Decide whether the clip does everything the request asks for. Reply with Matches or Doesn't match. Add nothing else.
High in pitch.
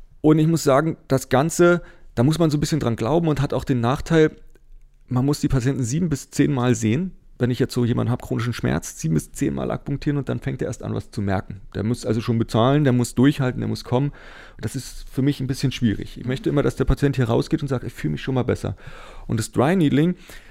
Doesn't match